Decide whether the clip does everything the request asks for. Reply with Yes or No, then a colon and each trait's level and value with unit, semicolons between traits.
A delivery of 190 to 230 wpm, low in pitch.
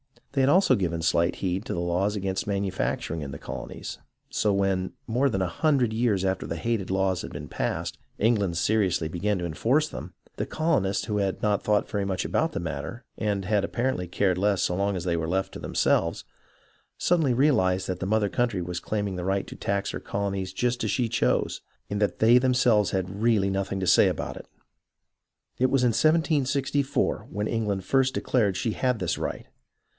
Yes: average, 200 wpm; low, 100 Hz